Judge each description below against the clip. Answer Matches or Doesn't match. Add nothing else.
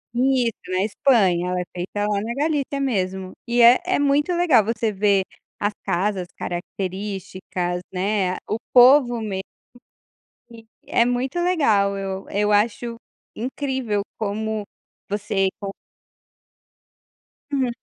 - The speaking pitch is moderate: Doesn't match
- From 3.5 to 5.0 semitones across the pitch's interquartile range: Matches